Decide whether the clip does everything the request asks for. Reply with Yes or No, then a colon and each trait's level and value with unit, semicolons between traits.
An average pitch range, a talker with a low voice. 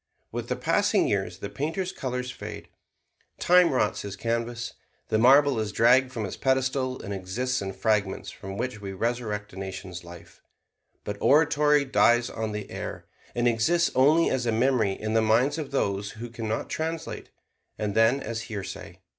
Yes: average, 4.2 semitones; low, 115 Hz